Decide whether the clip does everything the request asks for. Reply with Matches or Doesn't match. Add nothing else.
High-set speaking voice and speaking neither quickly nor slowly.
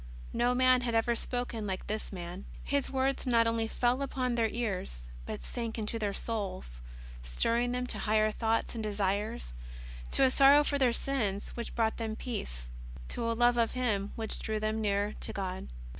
Matches